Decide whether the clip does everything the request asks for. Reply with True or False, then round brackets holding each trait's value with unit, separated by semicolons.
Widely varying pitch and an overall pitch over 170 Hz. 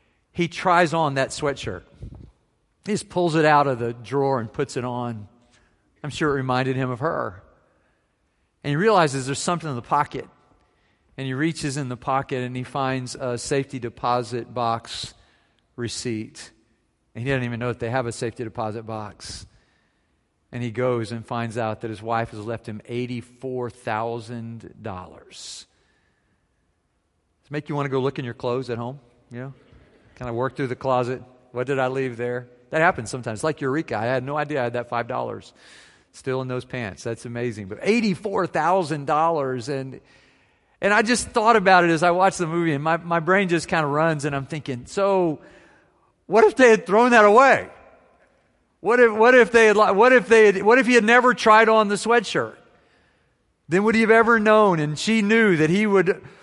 False (6.3 semitones; 135 Hz)